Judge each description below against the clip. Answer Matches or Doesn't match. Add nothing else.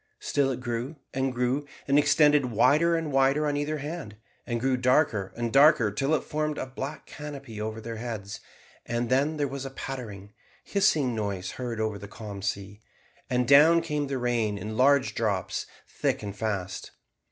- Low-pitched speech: Matches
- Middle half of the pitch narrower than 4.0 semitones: Doesn't match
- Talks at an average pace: Matches